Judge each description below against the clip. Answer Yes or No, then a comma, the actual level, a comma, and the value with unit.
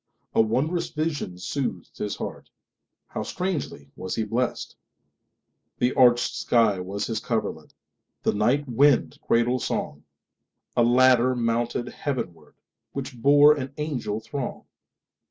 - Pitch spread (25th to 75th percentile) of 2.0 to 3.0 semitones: No, average, 4.1 semitones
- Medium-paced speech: No, slow, 100 wpm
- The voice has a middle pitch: No, low, 120 Hz